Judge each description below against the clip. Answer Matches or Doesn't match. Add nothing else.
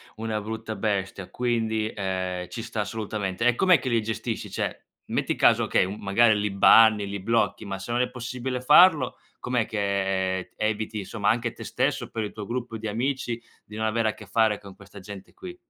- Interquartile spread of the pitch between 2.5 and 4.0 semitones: Matches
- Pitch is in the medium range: Doesn't match